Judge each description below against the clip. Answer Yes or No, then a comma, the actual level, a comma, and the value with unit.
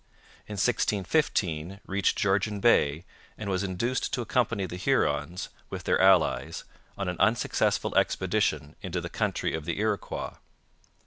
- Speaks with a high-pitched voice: No, very low, 95 Hz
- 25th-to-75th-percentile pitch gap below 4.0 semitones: Yes, average, 2.9 semitones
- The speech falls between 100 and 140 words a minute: Yes, slow, 135 wpm